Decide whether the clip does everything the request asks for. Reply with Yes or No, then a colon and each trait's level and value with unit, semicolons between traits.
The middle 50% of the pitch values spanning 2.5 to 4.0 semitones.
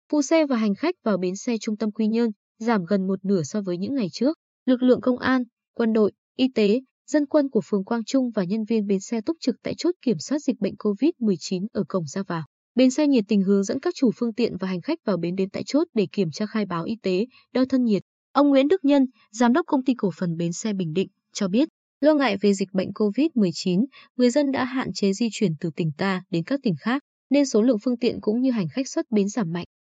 No: average, 4.8 semitones